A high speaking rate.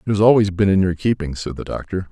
Yes: fast, 285 wpm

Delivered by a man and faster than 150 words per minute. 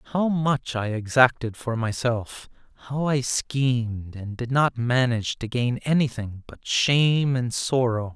No: male; average, 145 wpm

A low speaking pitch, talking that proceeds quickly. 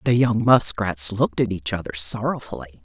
No: low, 100 Hz; average, 170 wpm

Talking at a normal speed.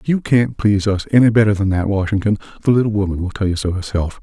No: fast, 240 wpm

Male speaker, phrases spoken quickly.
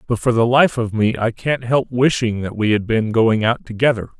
Yes: male; fast, 245 wpm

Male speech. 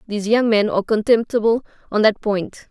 No: female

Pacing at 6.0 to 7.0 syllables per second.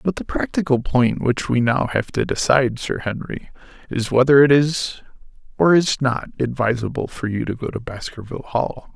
No: 5.1 syllables/s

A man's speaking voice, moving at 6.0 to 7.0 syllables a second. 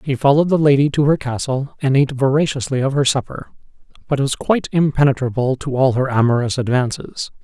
Yes: male; 6.1 syllables/s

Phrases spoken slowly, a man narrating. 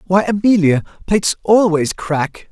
Yes: slow, 120 wpm; male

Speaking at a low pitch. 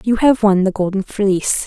No: high, 205 Hz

